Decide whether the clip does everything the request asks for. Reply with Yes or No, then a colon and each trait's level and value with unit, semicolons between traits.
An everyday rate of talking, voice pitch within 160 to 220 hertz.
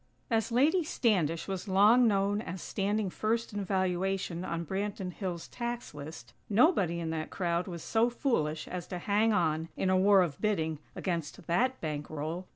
Yes: average, 165 wpm; high, 190 Hz